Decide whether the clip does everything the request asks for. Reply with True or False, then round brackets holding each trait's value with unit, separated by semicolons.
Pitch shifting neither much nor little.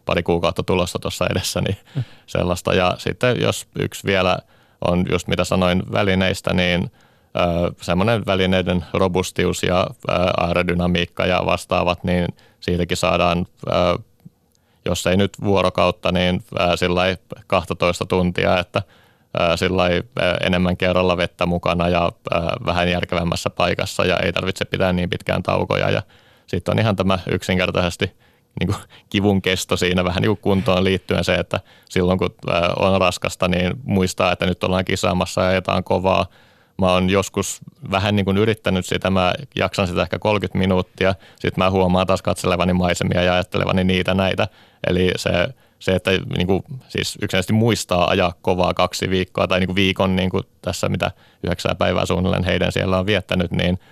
False (1.6 semitones)